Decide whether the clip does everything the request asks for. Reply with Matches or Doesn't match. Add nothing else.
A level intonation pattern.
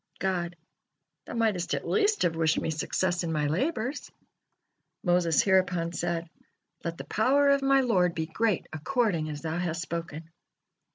Doesn't match